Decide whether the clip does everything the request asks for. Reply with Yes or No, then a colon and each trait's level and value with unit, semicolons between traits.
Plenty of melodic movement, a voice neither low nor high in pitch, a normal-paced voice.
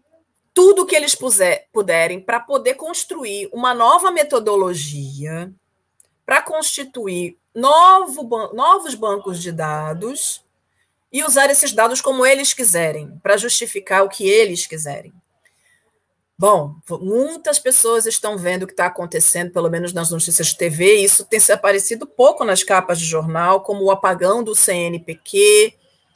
No: wide, 7.9 semitones; high, 210 Hz; average, 140 wpm